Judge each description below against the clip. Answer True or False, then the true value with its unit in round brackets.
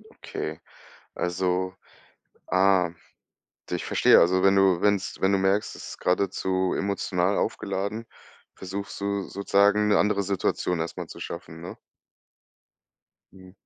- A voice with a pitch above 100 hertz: False (95 Hz)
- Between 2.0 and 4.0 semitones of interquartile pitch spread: False (1.5 semitones)